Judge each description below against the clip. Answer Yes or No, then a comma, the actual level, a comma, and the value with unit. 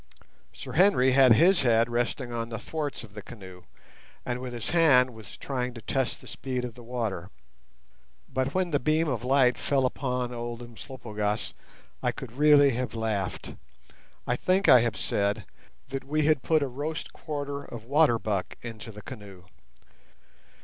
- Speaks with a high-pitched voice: No, low, 125 Hz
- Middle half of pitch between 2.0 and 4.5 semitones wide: Yes, average, 3.7 semitones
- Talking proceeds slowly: No, average, 170 wpm